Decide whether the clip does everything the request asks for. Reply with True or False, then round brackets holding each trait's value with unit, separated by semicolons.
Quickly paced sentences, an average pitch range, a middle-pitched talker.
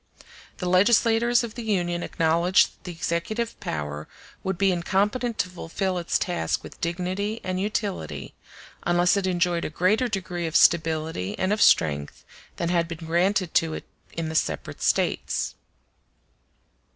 False (150 wpm; 3.2 semitones; 180 Hz)